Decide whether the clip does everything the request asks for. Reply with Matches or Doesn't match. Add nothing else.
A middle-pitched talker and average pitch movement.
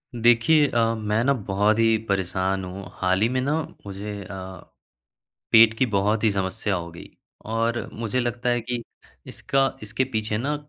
Doesn't match